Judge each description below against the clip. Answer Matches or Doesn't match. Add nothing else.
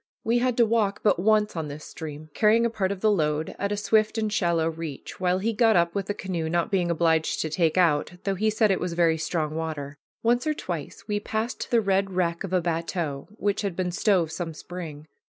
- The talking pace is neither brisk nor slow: Doesn't match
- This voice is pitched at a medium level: Matches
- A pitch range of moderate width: Matches